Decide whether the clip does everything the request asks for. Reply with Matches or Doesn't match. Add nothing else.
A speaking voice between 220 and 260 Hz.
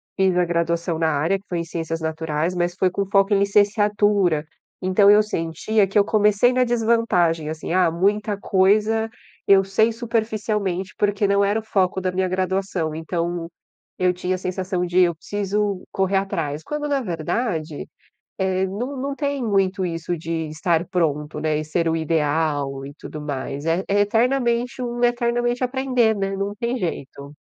Doesn't match